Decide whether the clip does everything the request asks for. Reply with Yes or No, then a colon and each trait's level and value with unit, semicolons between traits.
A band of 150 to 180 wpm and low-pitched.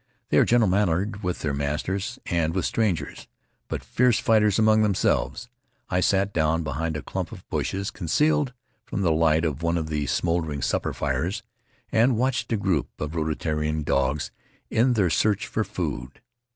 Yes: average, 170 wpm; very low, 90 Hz